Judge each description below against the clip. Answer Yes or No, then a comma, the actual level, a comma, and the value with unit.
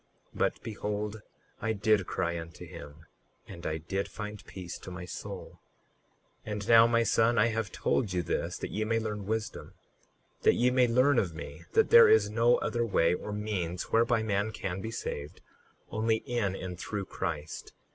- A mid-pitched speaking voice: No, low, 105 Hz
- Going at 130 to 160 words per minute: No, average, 180 wpm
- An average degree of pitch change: Yes, average, 3.9 semitones